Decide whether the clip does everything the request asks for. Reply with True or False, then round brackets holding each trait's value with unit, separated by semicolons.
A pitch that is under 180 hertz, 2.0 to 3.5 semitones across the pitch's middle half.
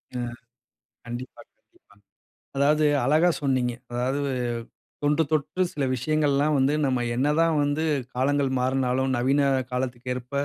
True (135 Hz; 2.7 semitones)